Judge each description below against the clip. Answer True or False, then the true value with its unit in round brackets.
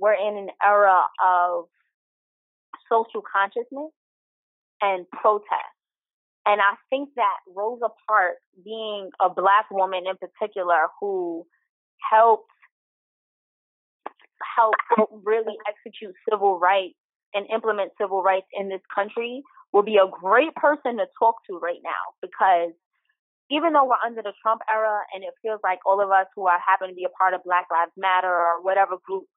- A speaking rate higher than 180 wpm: False (150 wpm)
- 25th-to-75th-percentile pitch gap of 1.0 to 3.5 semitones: True (3.1 semitones)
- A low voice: False (205 Hz)